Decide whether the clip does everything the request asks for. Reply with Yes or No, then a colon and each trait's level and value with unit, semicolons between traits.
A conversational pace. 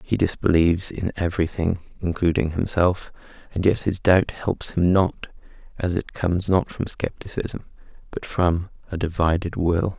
Yes: average, 145 wpm